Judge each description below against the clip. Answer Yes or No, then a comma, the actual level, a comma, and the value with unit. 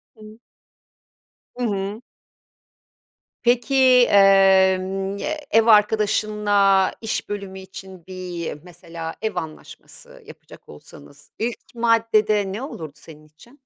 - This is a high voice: Yes, high, 200 Hz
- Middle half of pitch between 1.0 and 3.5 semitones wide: Yes, average, 2.9 semitones